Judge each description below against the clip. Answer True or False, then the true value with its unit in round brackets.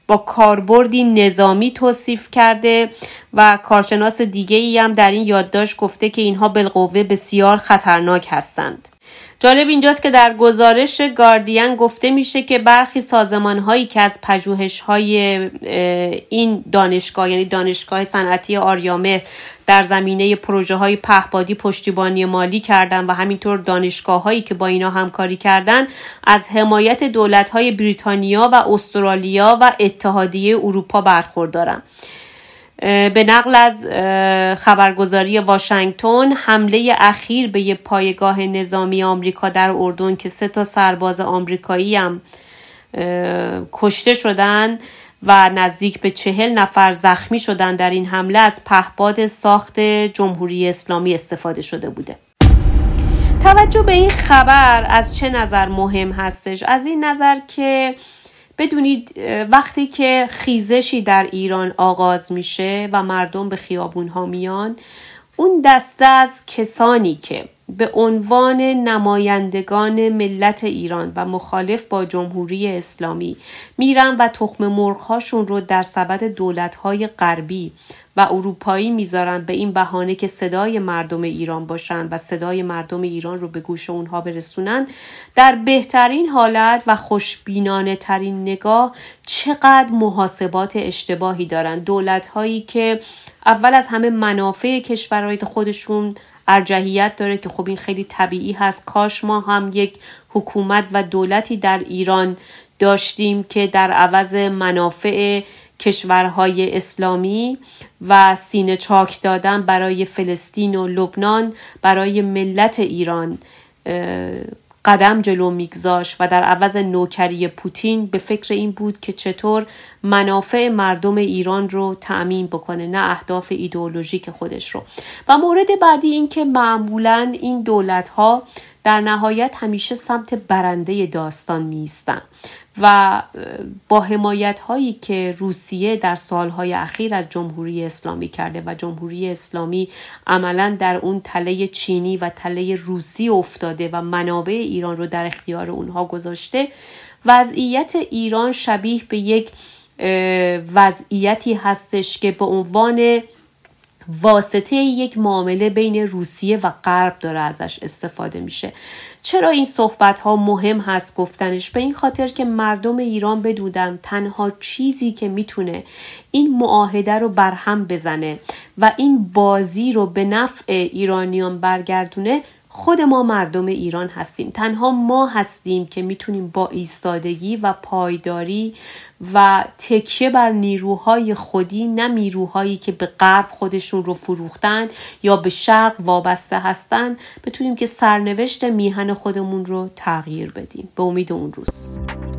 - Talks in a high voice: True (200 Hz)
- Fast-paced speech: False (125 wpm)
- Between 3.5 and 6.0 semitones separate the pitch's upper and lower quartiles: False (3.1 semitones)